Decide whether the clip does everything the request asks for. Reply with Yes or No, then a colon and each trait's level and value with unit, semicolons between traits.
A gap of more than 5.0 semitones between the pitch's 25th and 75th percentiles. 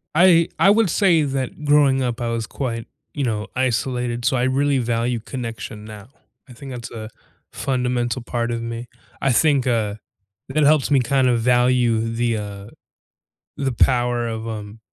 No: average, 2.7 semitones